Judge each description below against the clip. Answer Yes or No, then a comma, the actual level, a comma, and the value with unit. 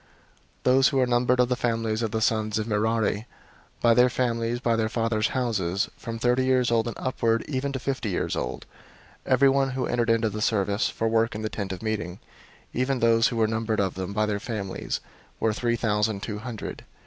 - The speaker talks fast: Yes, fast, 215 wpm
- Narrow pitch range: Yes, narrow, 2.3 semitones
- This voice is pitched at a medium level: No, low, 115 Hz